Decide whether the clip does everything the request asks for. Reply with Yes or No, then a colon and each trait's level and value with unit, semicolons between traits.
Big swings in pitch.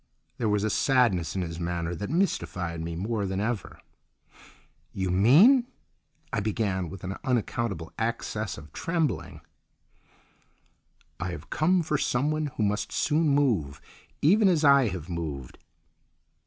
Yes: wide, 8.4 semitones